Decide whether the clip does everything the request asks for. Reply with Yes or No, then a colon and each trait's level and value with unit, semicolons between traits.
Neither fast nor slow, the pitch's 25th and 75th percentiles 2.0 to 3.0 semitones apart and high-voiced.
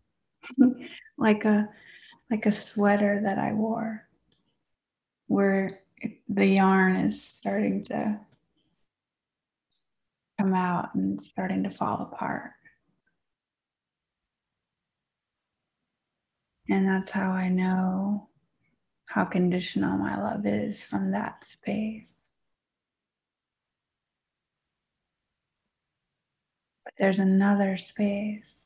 No: slow, 80 wpm; narrow, 2.5 semitones; high, 195 Hz